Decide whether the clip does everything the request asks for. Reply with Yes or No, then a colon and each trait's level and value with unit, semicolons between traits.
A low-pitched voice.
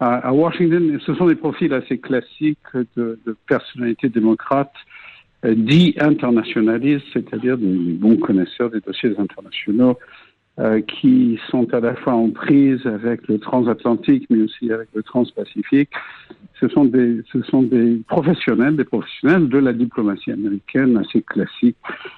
Yes: low, 125 Hz